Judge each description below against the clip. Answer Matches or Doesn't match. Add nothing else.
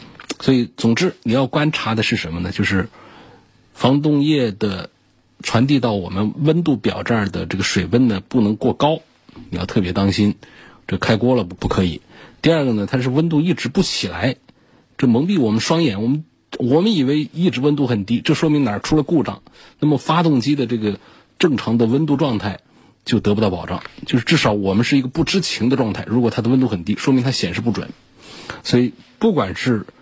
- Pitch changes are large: Matches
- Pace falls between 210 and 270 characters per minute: Doesn't match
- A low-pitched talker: Matches